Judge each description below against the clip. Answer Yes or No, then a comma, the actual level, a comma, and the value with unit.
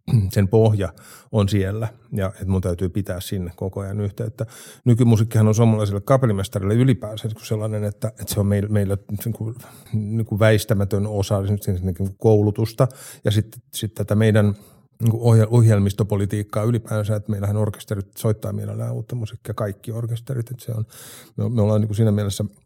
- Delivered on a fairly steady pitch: Yes, narrow, 2.0 semitones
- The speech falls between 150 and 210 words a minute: No, average, 130 wpm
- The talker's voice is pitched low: Yes, low, 110 Hz